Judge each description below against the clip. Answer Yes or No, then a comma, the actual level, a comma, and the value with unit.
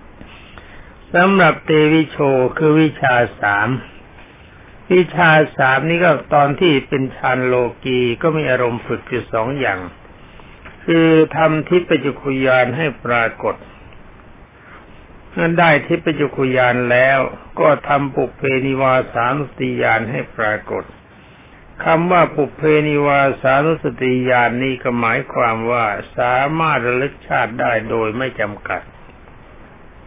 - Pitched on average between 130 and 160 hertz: Yes, low, 135 Hz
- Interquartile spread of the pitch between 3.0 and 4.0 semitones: Yes, average, 3.7 semitones